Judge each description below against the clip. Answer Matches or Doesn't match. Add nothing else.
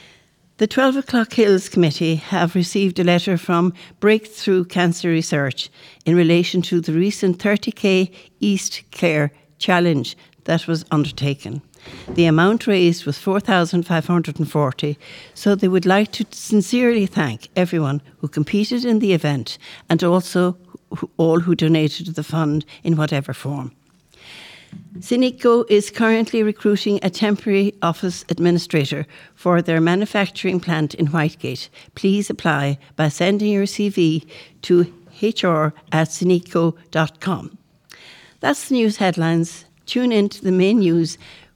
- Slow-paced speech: Matches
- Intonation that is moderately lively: Matches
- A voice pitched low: Doesn't match